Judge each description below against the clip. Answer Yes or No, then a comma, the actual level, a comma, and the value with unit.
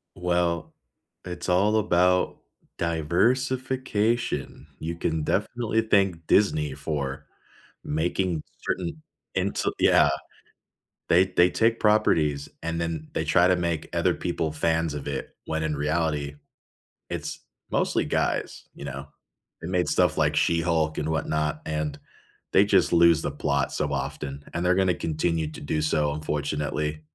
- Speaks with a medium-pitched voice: No, very low, 85 Hz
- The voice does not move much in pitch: No, average, 3.2 semitones